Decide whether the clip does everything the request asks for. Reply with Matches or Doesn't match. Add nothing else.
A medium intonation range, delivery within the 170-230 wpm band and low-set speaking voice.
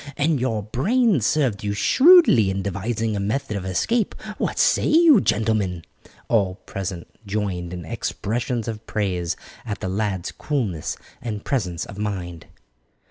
Doesn't match